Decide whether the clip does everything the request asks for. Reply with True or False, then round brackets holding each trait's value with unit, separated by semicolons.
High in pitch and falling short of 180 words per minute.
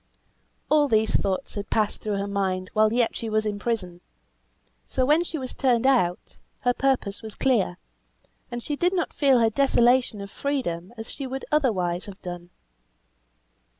True (225 Hz; 170 wpm)